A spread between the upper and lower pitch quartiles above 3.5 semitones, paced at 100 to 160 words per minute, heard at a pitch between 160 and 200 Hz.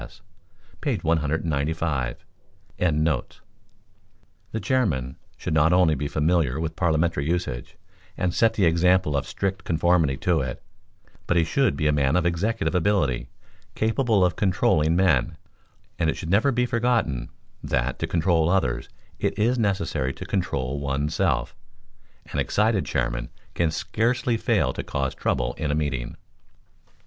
No: average, 5.2 semitones; average, 140 wpm; very low, 80 Hz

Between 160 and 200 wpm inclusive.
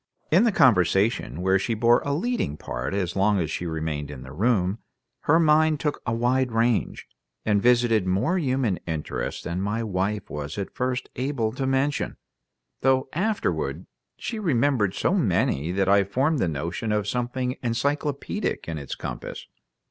Yes: average, 165 wpm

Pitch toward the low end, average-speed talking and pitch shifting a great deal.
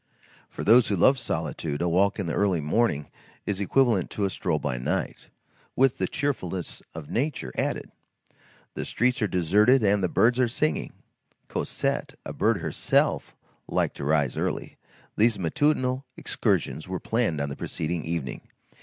Yes: low, 100 Hz; average, 160 wpm; wide, 6.9 semitones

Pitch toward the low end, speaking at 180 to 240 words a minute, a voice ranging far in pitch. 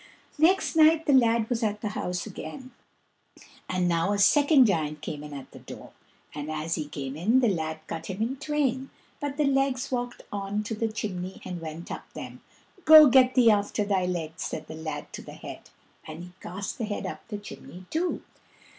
No: high, 205 Hz; average, 200 wpm; wide, 7.4 semitones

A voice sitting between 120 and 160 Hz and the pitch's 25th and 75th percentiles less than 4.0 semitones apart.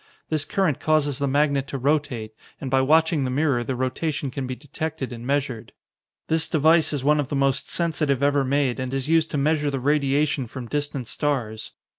Yes: medium, 140 Hz; narrow, 2.5 semitones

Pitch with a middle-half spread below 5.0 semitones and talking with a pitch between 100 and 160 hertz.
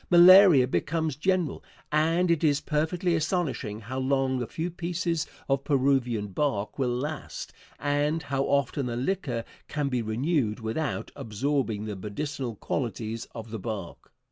No: average, 5.3 semitones; medium, 140 Hz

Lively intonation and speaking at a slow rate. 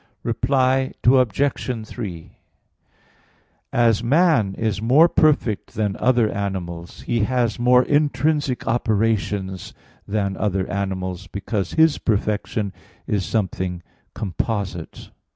No: average, 4.5 semitones; slow, 100 wpm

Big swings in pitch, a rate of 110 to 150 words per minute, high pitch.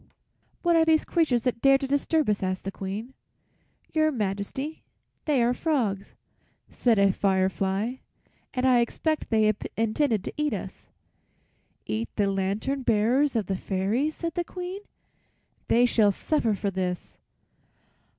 Yes: wide, 6.4 semitones; average, 145 wpm; high, 235 Hz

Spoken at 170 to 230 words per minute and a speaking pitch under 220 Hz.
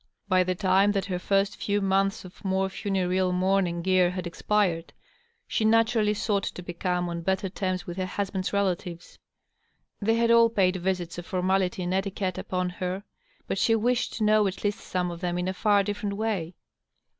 Yes: average, 185 wpm; high, 190 Hz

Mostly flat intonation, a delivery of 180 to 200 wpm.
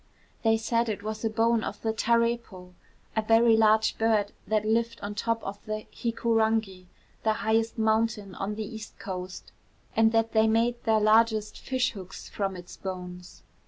No: narrow, 1.6 semitones; average, 165 wpm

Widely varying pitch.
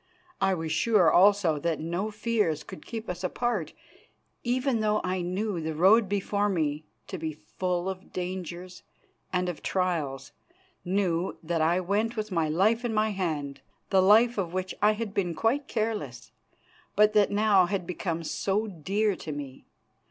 No: average, 4.1 semitones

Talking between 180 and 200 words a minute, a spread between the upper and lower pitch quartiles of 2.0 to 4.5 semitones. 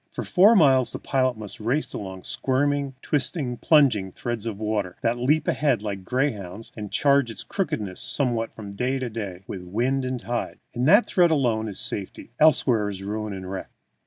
No: average, 190 wpm; average, 4.9 semitones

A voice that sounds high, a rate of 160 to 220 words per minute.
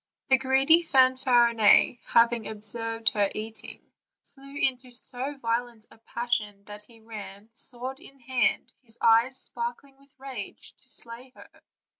No: high, 240 Hz; average, 140 wpm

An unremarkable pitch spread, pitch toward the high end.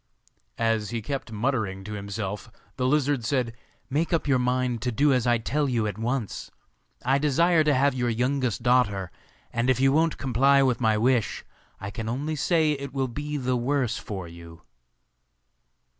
No: average, 3.8 semitones; low, 125 Hz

